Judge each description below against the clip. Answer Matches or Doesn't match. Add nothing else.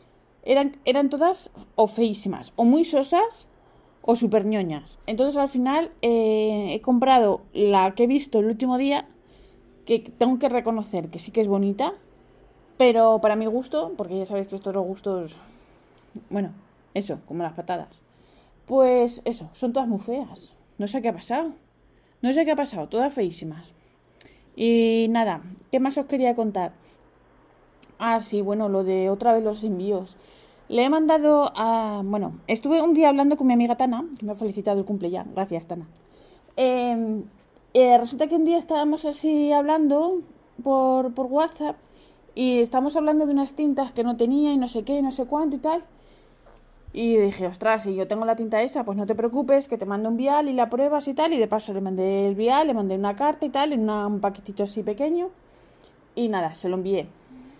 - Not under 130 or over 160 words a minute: Doesn't match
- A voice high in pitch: Matches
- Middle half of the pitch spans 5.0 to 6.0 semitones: Matches